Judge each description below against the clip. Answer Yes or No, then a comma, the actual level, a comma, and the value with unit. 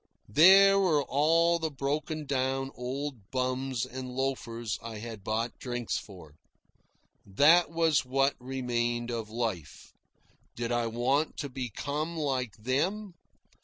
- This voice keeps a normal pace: No, slow, 125 wpm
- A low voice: Yes, low, 130 Hz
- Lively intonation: No, average, 3.9 semitones